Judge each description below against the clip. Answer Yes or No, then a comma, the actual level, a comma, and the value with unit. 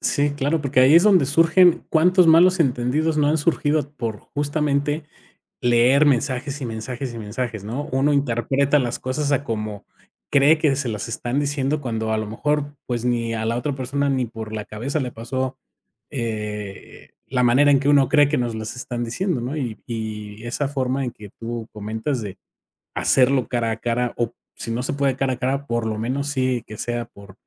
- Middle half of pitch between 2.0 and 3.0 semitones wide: No, average, 3.7 semitones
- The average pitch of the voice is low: Yes, low, 130 Hz